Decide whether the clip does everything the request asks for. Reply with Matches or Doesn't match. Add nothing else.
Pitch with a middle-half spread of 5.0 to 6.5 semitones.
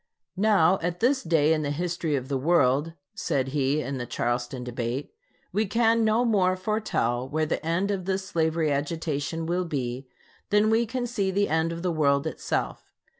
Matches